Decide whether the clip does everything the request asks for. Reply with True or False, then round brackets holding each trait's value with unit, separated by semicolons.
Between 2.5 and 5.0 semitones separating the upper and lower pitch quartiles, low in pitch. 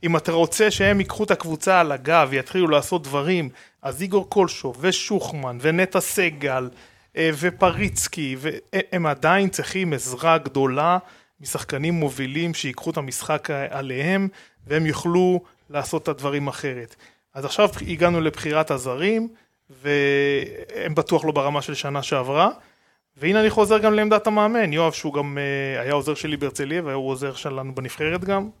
False (4.6 semitones; 155 Hz)